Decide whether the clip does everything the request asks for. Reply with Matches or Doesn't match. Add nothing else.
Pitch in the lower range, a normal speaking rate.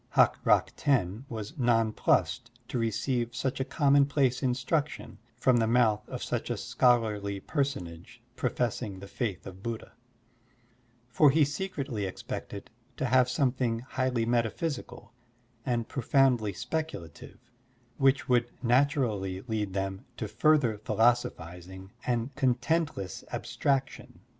Doesn't match